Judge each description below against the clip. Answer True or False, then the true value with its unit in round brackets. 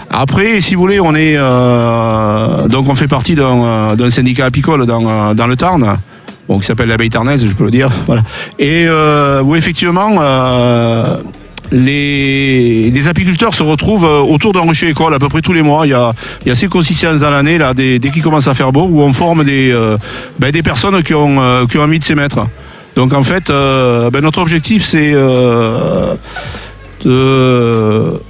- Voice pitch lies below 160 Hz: True (140 Hz)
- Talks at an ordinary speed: True (205 wpm)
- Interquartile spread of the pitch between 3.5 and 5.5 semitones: True (4.7 semitones)